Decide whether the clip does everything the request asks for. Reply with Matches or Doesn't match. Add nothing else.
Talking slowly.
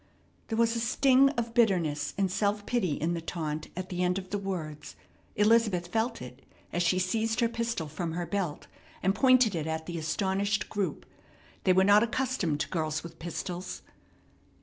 Doesn't match